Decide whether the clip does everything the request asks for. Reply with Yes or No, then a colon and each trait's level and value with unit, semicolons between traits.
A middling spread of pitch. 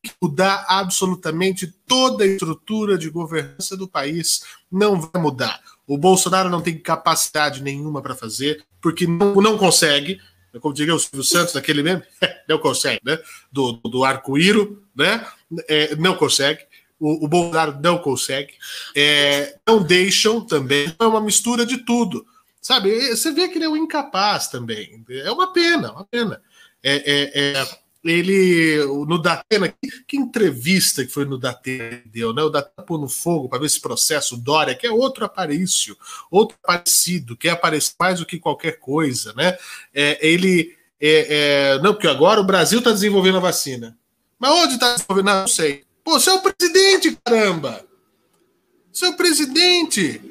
No: wide, 6.3 semitones